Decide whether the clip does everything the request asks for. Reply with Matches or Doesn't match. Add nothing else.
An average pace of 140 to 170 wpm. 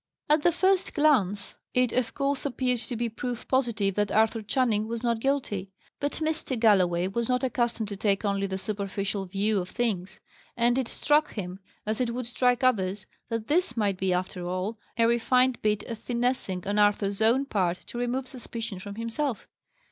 Doesn't match